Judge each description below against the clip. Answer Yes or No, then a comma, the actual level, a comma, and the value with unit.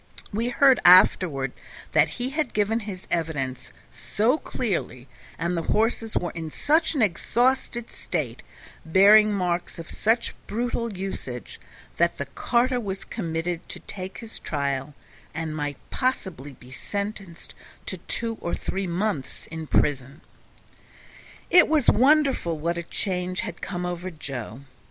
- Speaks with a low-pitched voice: No, medium, 185 Hz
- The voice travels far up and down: Yes, wide, 6.0 semitones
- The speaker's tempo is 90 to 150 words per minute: Yes, slow, 135 wpm